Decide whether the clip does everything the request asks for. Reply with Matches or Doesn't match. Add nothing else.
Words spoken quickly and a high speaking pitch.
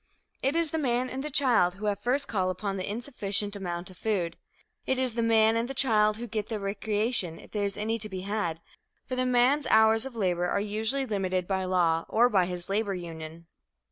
Matches